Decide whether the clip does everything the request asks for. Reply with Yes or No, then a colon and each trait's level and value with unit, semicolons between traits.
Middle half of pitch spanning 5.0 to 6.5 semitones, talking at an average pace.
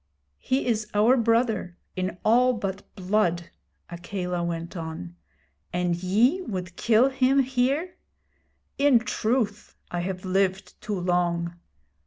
No: average, 5.3 semitones; slow, 120 wpm